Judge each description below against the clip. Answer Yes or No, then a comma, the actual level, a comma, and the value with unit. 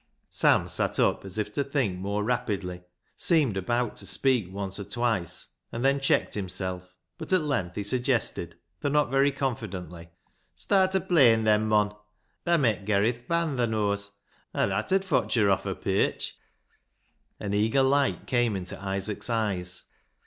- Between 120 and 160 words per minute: No, average, 175 wpm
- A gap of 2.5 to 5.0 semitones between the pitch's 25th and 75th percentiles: No, wide, 5.5 semitones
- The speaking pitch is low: Yes, low, 110 Hz